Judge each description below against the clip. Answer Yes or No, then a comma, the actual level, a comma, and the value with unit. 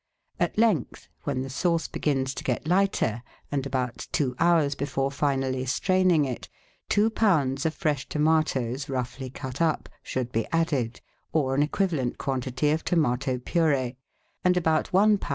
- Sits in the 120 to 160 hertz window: Yes, medium, 140 Hz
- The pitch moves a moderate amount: Yes, average, 4.0 semitones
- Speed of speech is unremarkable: Yes, average, 155 wpm